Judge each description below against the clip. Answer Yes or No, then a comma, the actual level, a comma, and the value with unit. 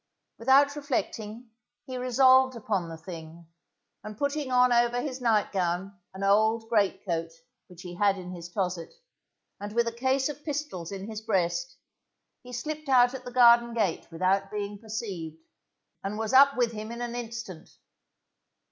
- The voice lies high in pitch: Yes, high, 225 Hz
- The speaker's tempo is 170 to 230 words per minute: No, average, 160 wpm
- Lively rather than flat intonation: No, average, 4.6 semitones